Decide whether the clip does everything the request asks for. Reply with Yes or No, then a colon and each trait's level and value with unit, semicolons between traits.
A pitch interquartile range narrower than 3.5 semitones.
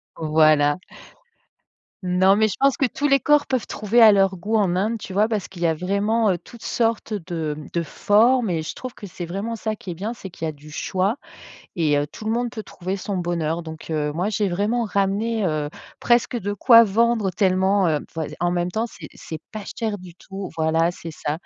No: average, 4.6 semitones